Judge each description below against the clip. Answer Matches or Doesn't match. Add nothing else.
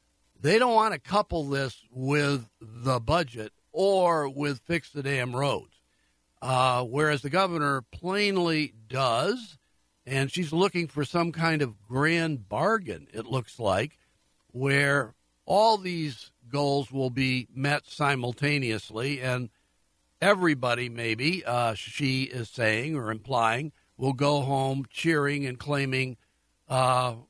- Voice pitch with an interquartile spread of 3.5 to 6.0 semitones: Matches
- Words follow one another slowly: Matches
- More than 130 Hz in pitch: Matches